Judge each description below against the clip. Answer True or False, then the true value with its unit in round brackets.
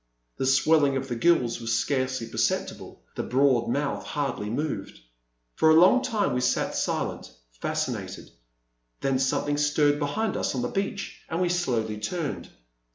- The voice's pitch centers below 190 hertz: True (135 Hz)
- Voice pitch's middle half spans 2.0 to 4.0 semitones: False (4.7 semitones)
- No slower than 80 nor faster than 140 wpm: False (155 wpm)